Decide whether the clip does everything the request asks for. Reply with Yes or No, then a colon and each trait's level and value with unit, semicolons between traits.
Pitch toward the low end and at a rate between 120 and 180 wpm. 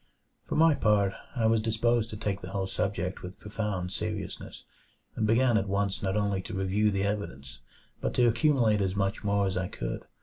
No: low, 100 Hz; average, 195 wpm